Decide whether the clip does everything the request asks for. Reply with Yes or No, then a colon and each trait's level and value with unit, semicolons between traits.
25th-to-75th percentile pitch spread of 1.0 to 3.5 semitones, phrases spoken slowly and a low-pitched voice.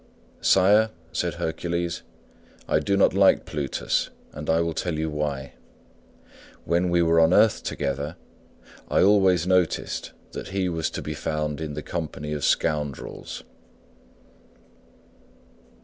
Yes: average, 3.1 semitones; slow, 130 wpm; very low, 80 Hz